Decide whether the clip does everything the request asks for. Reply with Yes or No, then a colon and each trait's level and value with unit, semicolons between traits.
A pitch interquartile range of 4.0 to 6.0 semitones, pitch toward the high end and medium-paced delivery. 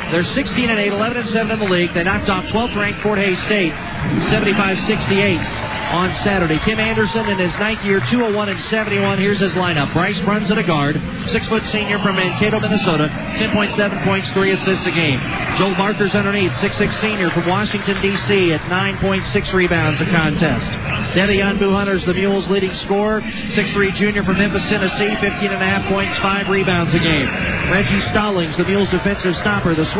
No: narrow, 2.4 semitones; high, 195 Hz; average, 160 wpm